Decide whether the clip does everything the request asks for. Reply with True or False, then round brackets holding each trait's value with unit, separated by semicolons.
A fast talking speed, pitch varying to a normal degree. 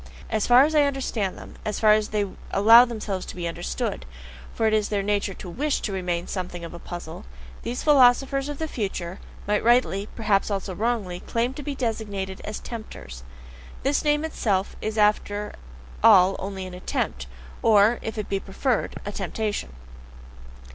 False (175 wpm; 3.8 semitones)